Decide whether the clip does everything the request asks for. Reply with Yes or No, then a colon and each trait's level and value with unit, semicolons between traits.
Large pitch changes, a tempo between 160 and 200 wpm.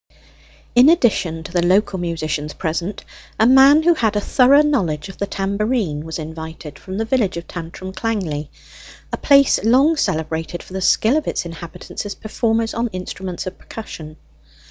Yes: wide, 5.8 semitones; average, 165 wpm